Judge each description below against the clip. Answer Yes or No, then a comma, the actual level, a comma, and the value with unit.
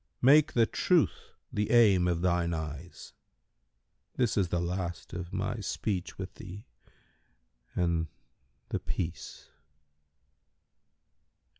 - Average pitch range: Yes, average, 3.6 semitones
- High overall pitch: No, very low, 90 Hz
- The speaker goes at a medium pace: No, slow, 100 wpm